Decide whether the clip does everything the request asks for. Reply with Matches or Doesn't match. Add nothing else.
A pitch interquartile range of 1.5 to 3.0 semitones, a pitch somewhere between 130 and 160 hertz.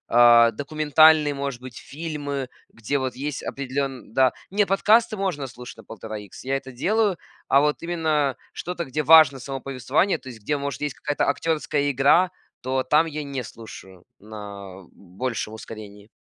Doesn't match